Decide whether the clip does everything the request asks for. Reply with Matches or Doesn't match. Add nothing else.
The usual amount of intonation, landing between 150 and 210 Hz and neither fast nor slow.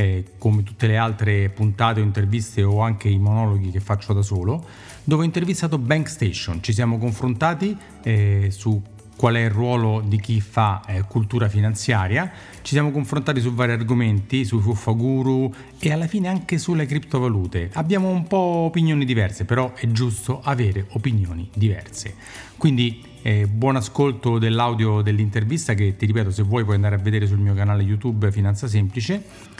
Doesn't match